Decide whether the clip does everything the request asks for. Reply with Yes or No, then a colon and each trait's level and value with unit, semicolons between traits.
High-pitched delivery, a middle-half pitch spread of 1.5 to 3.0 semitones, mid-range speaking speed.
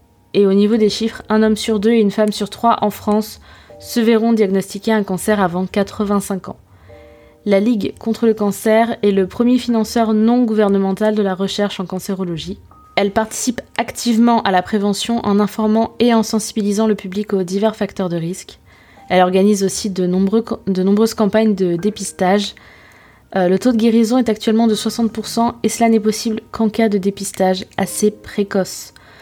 Yes: high, 210 Hz; narrow, 2.6 semitones; average, 180 wpm